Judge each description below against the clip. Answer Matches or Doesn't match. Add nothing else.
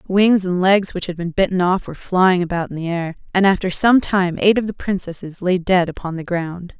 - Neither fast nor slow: Doesn't match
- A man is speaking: Doesn't match